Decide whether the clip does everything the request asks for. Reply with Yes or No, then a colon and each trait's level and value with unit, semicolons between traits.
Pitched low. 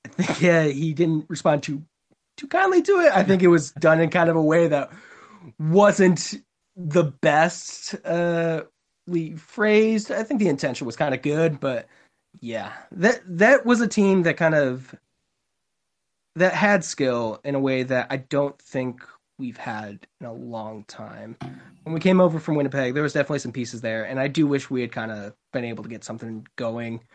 No: medium, 160 Hz